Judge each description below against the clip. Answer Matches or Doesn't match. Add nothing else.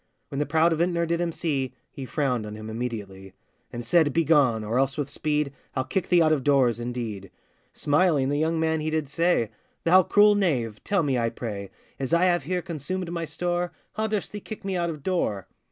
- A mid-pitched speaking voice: Matches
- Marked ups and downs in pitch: Matches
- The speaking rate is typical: Doesn't match